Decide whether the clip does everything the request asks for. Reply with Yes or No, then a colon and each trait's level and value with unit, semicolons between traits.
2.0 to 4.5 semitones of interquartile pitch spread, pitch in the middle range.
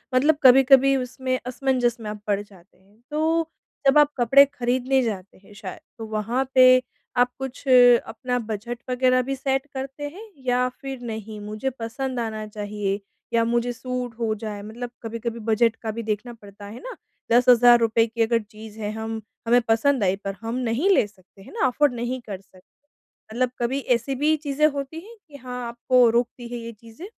No: average, 3.0 semitones; high, 240 Hz